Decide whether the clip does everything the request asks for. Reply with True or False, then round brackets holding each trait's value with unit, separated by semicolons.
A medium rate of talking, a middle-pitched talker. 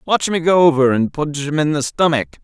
False (245 wpm; 155 Hz)